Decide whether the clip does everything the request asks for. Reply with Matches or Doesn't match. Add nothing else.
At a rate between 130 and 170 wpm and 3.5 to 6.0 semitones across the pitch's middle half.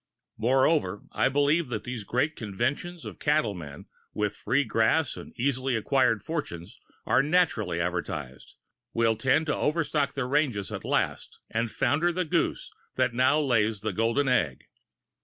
Matches